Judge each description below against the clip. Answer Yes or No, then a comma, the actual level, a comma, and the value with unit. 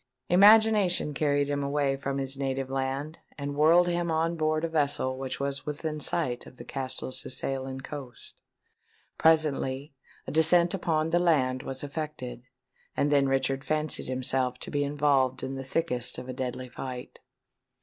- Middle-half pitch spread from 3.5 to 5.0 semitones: No, average, 2.9 semitones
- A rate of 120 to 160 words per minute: Yes, average, 155 wpm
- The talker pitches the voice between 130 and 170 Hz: Yes, medium, 140 Hz